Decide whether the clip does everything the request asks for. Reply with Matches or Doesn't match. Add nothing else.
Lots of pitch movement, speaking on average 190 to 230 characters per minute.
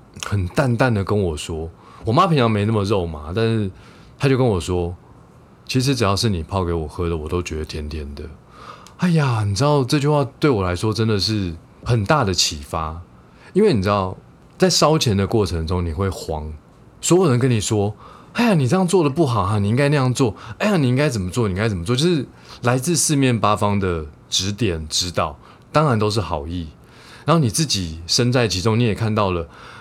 Doesn't match